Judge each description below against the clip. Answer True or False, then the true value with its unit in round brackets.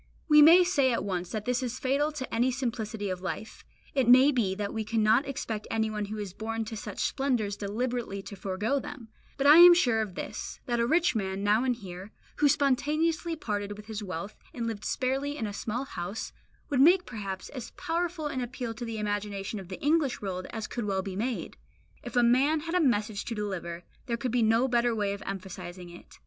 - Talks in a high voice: True (225 Hz)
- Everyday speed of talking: False (215 wpm)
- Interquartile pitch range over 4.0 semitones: True (4.6 semitones)